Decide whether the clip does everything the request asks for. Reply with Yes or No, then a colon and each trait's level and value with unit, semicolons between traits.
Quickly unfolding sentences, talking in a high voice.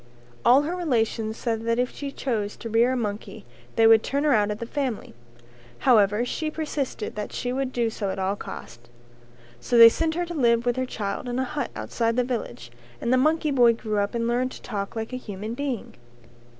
Yes: fast, 215 wpm; high, 235 Hz